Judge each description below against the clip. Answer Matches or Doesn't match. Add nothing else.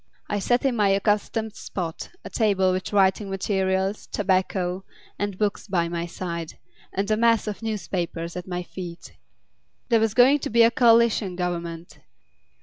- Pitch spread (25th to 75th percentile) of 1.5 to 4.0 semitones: Matches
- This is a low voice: Doesn't match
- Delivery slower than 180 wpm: Matches